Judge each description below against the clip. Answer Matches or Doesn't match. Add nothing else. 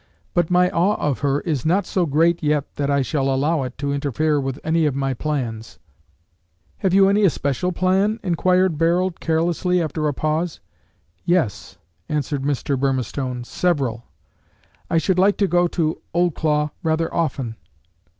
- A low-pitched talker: Doesn't match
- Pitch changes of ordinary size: Matches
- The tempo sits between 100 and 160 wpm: Matches